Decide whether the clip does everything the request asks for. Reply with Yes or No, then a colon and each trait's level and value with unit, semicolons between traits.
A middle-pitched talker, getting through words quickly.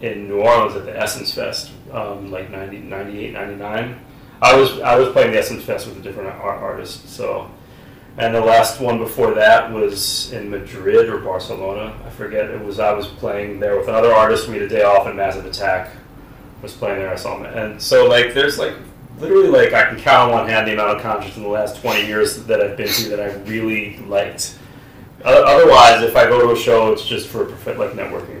No: low, 125 Hz; fast, 220 wpm